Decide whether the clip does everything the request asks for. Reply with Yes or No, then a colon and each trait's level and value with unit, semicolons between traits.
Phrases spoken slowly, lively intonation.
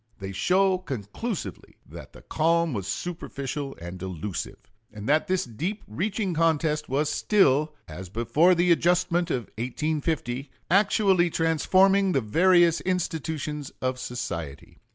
Yes: slow, 125 wpm; wide, 6.5 semitones